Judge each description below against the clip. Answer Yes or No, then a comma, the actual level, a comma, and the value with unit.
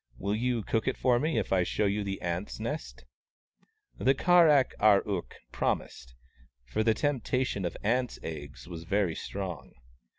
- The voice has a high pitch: No, low, 105 Hz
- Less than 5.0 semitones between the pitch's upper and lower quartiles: No, wide, 5.6 semitones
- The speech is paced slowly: No, average, 185 wpm